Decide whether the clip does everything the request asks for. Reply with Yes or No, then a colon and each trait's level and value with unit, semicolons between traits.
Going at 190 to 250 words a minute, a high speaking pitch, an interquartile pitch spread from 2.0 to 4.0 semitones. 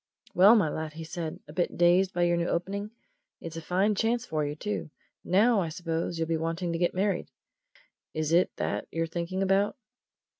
No: average, 195 wpm; medium, 175 Hz; average, 2.9 semitones